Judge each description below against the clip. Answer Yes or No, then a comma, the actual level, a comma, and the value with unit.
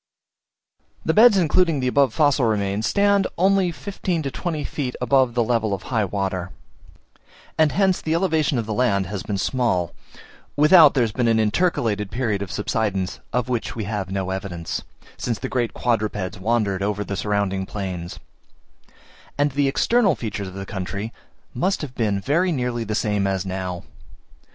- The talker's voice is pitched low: Yes, low, 115 Hz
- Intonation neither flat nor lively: No, wide, 6.5 semitones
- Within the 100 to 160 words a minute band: No, average, 175 wpm